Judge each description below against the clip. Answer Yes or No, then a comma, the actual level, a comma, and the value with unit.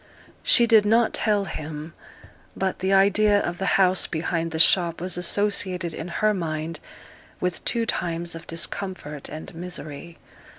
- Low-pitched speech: No, medium, 180 Hz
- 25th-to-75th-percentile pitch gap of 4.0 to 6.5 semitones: No, average, 3.2 semitones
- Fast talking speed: No, average, 145 wpm